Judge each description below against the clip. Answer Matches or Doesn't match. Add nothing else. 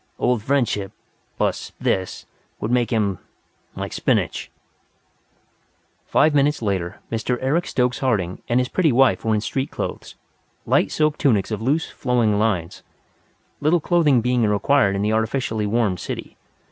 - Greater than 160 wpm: Doesn't match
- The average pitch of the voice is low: Matches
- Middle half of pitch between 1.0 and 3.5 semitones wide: Doesn't match